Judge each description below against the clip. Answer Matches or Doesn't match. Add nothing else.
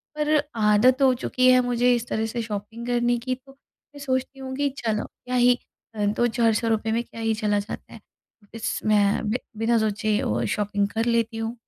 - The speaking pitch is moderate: Doesn't match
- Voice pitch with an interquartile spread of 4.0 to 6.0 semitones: Doesn't match